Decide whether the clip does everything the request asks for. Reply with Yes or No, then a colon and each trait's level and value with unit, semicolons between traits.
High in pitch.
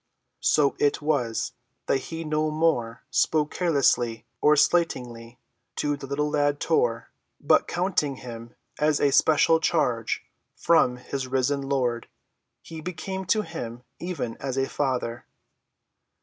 No: medium, 140 Hz